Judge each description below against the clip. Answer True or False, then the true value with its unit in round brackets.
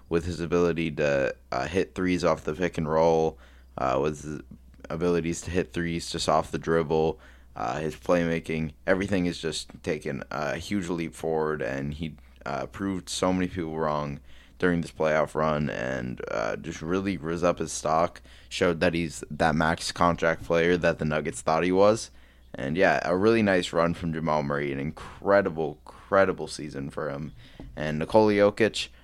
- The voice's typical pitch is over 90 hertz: False (80 Hz)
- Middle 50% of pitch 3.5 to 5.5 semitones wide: False (2.7 semitones)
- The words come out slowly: False (175 wpm)